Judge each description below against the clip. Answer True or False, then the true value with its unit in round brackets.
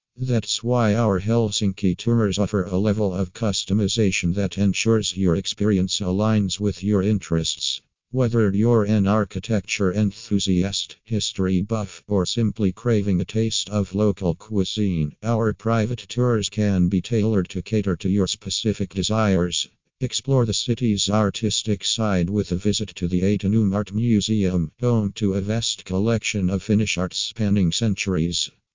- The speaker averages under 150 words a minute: True (140 wpm)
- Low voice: True (100 Hz)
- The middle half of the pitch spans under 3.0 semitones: True (2.5 semitones)